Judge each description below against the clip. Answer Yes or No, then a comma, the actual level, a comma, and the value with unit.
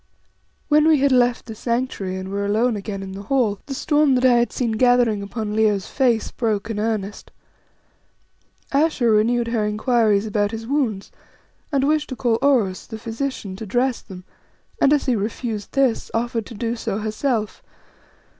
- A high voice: Yes, high, 230 Hz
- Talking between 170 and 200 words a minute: Yes, average, 175 wpm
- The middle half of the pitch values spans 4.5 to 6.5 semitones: No, average, 3.5 semitones